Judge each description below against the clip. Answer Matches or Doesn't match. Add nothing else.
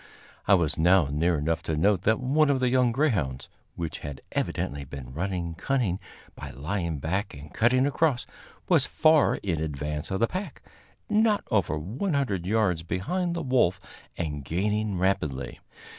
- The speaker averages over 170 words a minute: Doesn't match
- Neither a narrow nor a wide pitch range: Doesn't match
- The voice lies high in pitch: Doesn't match